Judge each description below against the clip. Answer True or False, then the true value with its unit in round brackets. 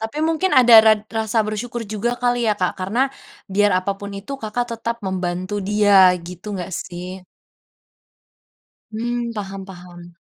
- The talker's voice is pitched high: True (210 Hz)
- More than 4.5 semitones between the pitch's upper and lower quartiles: False (3.9 semitones)